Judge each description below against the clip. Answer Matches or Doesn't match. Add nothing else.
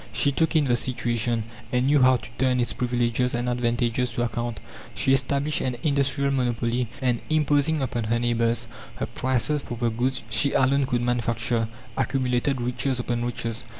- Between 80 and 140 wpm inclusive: Doesn't match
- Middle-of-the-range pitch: Doesn't match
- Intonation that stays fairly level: Matches